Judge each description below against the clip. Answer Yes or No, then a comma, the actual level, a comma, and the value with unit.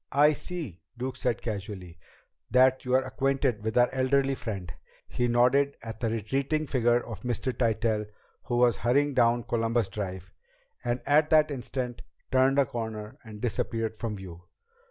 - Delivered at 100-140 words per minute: No, average, 155 wpm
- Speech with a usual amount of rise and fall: Yes, average, 3.1 semitones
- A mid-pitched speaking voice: No, low, 120 Hz